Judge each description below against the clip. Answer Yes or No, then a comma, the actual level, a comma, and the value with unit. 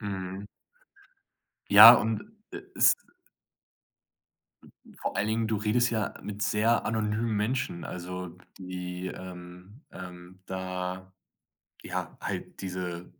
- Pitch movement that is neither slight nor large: Yes, average, 3.0 semitones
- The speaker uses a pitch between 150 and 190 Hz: No, very low, 95 Hz